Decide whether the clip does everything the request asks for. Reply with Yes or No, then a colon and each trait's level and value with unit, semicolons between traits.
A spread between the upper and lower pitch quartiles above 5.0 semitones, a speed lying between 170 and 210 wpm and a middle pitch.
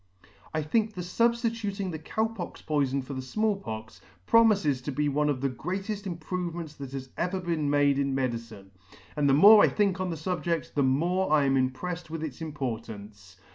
Yes: wide, 5.6 semitones; average, 195 wpm; medium, 155 Hz